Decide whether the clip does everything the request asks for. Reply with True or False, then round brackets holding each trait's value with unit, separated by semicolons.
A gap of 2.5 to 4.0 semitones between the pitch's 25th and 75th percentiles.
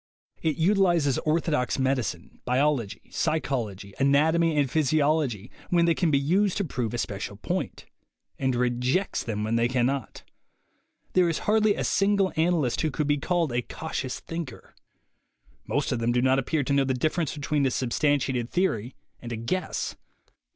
False (4.8 semitones)